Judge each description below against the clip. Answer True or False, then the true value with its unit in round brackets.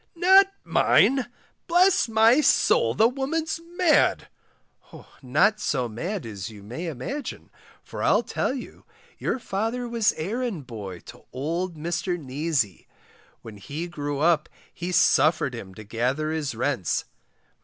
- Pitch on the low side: False (165 Hz)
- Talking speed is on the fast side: False (135 wpm)